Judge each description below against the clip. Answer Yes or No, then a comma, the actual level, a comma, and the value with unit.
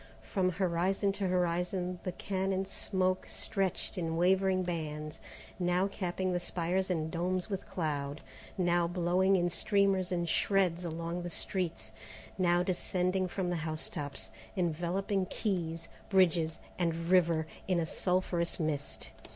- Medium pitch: Yes, medium, 180 Hz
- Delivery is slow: Yes, slow, 130 wpm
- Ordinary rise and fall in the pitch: No, narrow, 1.9 semitones